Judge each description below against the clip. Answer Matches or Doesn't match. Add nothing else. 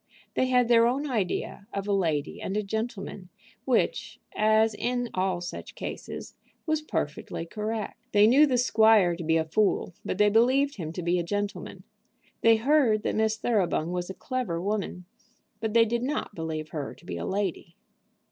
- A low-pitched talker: Doesn't match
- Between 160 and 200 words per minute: Matches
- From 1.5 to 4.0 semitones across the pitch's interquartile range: Doesn't match